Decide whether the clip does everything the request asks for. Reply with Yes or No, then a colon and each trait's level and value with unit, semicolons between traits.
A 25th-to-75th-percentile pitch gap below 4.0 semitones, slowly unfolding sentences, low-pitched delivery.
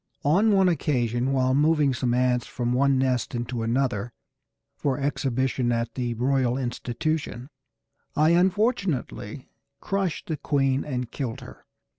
Yes: average, 3.6 semitones; slow, 130 wpm; low, 130 Hz